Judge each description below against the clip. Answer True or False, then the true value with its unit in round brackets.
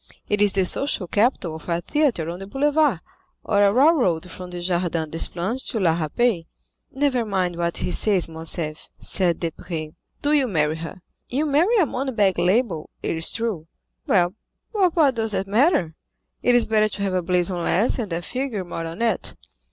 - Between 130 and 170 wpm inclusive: False (190 wpm)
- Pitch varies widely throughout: True (6.3 semitones)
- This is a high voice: True (195 Hz)